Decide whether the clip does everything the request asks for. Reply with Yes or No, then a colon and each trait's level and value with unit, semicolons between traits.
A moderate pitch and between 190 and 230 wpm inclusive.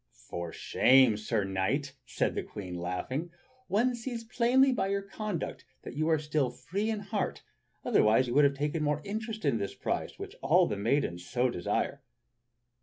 No: medium, 145 Hz; average, 180 wpm